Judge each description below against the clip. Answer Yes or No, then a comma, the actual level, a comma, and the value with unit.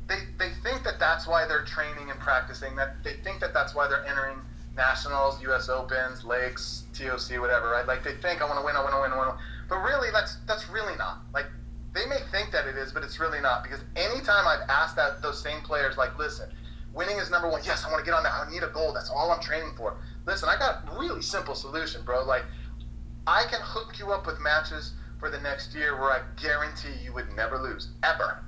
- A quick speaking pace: Yes, fast, 240 wpm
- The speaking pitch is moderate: No, low, 130 Hz